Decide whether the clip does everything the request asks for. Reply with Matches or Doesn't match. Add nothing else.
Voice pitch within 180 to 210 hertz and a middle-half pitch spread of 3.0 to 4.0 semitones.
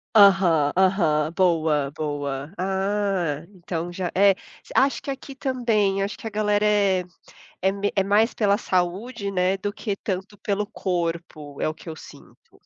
Matches